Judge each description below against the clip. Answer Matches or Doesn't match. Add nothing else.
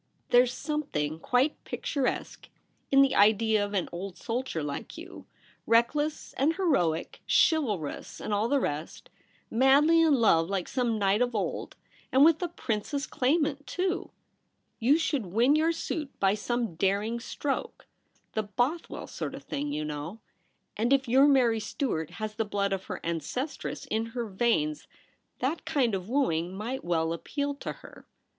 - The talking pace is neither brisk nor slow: Matches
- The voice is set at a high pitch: Matches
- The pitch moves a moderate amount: Doesn't match